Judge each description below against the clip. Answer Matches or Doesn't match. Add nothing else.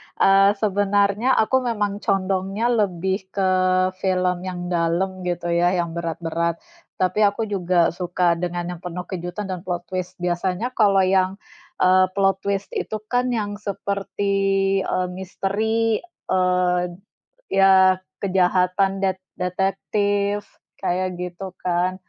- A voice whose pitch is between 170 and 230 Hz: Matches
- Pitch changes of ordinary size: Doesn't match